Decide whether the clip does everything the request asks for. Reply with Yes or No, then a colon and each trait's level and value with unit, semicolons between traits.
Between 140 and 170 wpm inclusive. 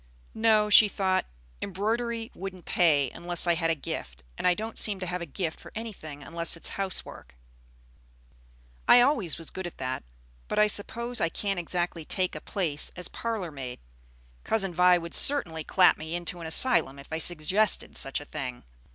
No: average, 185 wpm